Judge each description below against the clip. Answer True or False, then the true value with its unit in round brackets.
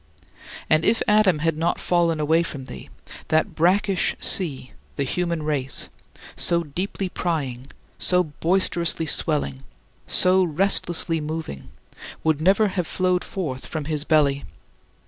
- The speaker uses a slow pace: True (125 wpm)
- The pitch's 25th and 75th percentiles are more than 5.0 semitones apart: False (3.2 semitones)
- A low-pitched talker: False (165 Hz)